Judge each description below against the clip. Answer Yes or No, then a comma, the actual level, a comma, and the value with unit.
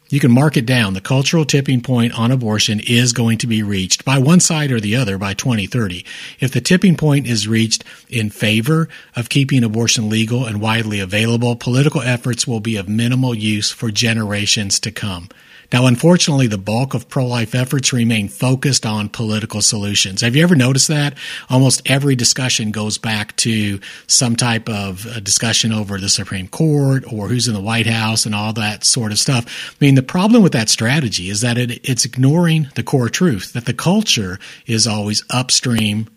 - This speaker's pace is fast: No, average, 190 wpm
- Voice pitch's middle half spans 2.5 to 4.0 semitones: Yes, average, 3.6 semitones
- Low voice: Yes, low, 120 Hz